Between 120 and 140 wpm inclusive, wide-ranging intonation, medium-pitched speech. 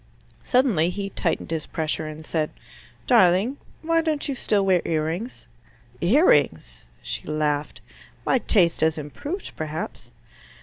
Yes: slow, 135 wpm; wide, 7.8 semitones; medium, 170 Hz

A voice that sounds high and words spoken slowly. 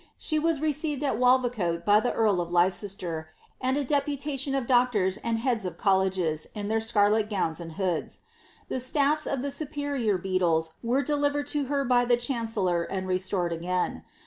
No: high, 225 Hz; average, 175 wpm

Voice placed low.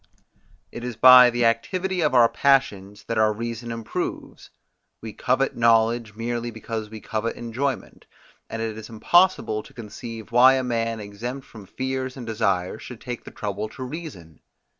Yes: low, 115 Hz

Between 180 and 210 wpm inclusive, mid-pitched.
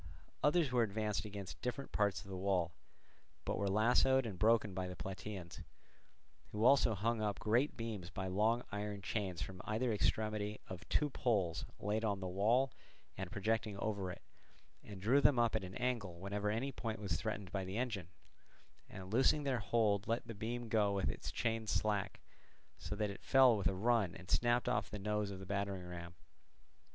No: average, 185 wpm; low, 105 Hz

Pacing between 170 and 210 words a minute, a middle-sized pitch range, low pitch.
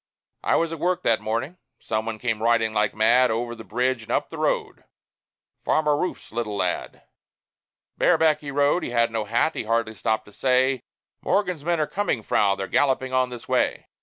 Yes: average, 190 wpm; average, 4.6 semitones; low, 120 Hz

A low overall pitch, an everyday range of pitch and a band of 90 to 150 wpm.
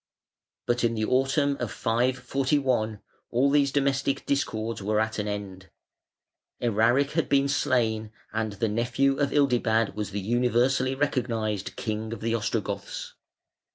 Yes: low, 120 Hz; average, 3.8 semitones; slow, 135 wpm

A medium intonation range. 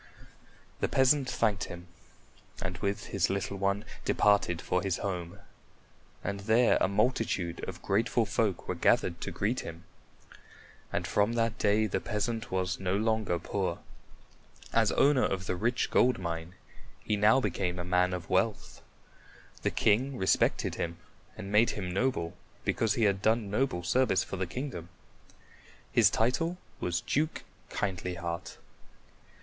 Yes: average, 3.9 semitones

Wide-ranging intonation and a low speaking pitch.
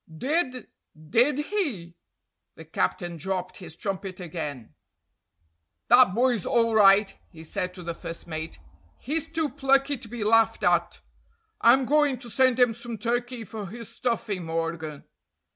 No: wide, 6.2 semitones; high, 225 Hz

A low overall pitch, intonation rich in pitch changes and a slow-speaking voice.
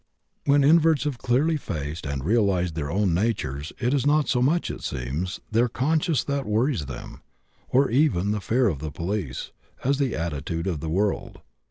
No: low, 105 Hz; wide, 9.0 semitones; average, 180 wpm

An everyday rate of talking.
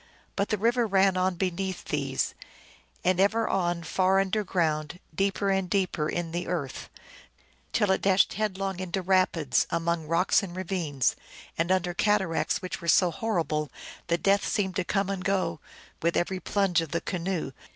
Yes: average, 165 wpm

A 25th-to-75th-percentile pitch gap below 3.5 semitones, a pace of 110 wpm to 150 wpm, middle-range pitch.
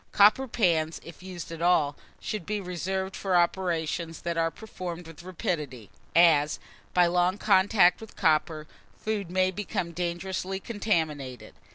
Yes: narrow, 2.6 semitones; average, 140 wpm; medium, 175 Hz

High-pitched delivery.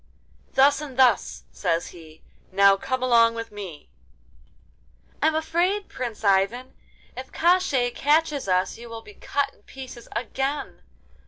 Yes: very high, 255 Hz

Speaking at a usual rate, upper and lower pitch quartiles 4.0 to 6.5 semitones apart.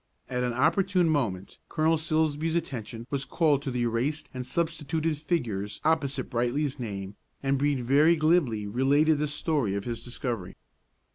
Yes: average, 150 wpm; average, 4.6 semitones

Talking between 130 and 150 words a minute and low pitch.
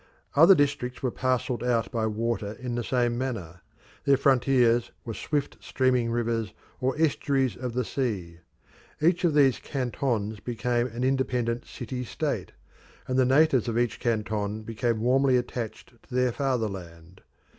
Yes: average, 145 wpm; low, 120 Hz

